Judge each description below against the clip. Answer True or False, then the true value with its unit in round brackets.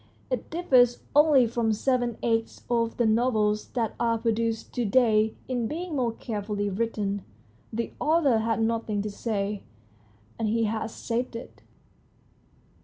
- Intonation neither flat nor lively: False (2.1 semitones)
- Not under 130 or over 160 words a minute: True (140 wpm)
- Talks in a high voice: True (230 Hz)